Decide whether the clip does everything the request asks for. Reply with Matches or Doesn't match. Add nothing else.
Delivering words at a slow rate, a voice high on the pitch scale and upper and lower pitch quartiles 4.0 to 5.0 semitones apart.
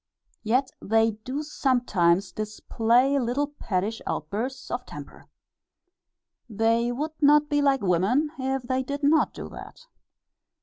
Matches